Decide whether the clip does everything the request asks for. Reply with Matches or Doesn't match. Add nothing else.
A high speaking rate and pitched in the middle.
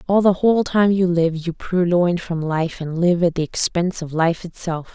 Matches